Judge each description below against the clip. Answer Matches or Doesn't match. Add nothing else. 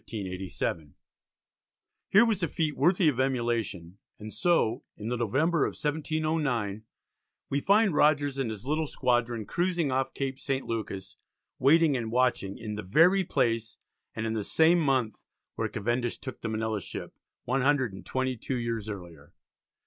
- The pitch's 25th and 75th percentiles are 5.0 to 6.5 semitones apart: Matches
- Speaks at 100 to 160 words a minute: Matches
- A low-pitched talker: Matches